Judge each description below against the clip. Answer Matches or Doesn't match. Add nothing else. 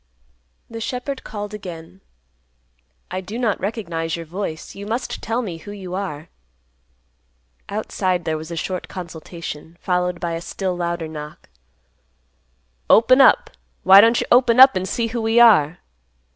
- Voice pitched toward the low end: Doesn't match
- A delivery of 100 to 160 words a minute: Matches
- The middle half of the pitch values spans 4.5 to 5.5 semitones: Matches